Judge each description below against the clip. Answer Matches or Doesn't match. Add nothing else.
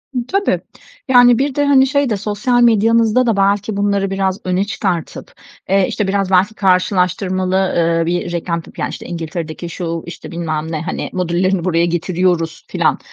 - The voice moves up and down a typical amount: Matches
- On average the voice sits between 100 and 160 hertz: Doesn't match